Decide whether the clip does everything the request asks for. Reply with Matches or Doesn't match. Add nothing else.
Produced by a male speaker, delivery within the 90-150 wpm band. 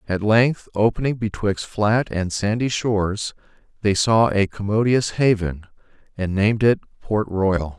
Matches